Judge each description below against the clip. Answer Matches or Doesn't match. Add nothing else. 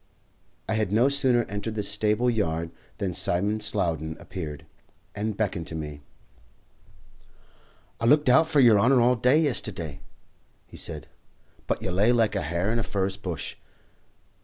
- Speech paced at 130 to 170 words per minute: Matches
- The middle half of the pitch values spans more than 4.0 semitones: Matches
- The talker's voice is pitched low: Matches